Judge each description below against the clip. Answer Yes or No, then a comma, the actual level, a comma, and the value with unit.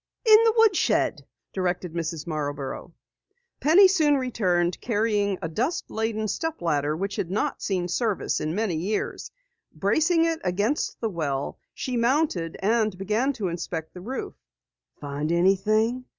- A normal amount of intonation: No, wide, 6.6 semitones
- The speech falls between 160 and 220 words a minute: No, average, 140 wpm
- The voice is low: No, high, 205 Hz